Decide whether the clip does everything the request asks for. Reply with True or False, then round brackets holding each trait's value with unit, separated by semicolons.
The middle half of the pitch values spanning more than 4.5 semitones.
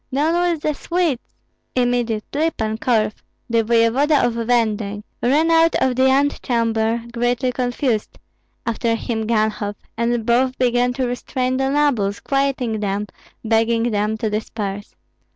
False (3.0 semitones)